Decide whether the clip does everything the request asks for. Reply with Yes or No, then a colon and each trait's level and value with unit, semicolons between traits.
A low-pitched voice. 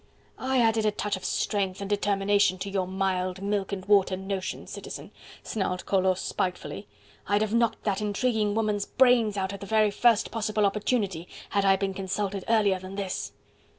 No: high, 200 Hz